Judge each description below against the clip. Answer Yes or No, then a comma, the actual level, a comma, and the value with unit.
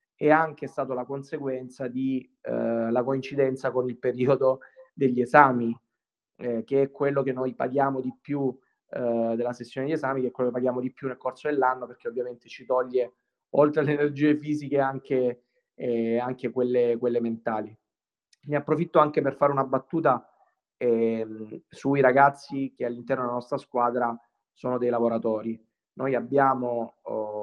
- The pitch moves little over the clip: Yes, narrow, 2.3 semitones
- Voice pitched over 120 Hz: Yes, low, 130 Hz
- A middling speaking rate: Yes, average, 160 wpm